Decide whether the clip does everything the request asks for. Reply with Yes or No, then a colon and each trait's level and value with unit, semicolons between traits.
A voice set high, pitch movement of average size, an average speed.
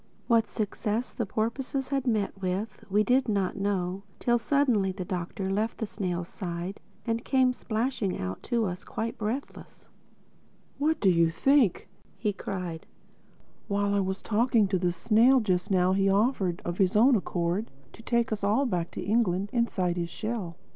Yes: high, 205 Hz; average, 4.1 semitones; average, 170 wpm